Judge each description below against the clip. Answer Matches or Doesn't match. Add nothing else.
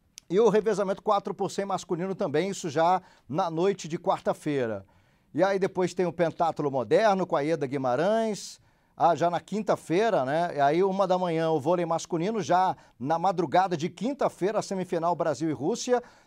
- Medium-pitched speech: Matches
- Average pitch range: Matches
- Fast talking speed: Doesn't match